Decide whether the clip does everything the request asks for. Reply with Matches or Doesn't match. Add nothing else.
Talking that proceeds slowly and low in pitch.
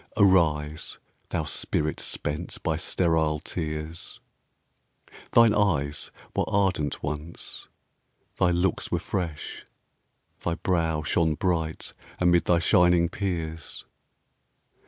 Matches